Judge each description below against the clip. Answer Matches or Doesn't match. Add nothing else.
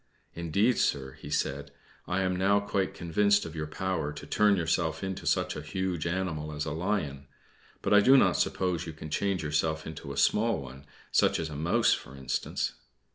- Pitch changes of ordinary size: Matches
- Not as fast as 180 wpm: Doesn't match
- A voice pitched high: Doesn't match